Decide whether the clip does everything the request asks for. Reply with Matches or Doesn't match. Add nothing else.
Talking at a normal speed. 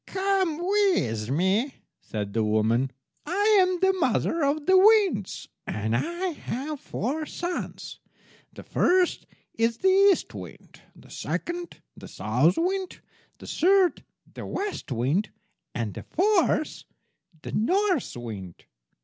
Doesn't match